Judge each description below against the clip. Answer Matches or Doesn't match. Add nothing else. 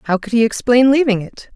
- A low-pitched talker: Doesn't match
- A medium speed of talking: Doesn't match